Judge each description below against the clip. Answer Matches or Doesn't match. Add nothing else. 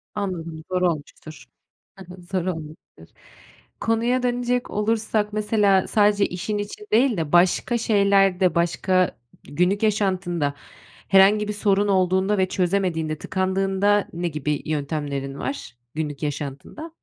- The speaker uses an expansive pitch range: Doesn't match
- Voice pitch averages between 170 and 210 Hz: Matches